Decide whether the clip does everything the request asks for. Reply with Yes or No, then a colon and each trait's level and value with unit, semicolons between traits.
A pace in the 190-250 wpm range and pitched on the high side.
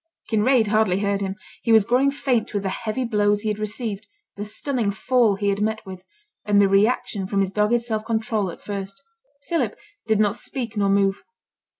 Yes: average, 195 wpm; high, 210 Hz